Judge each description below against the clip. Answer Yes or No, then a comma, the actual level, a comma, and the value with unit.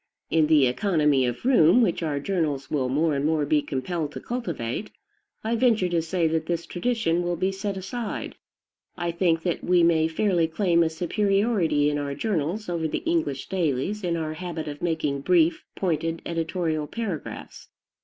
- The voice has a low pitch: No, medium, 165 Hz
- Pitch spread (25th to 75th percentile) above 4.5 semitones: No, average, 3.7 semitones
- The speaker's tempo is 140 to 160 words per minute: No, average, 175 wpm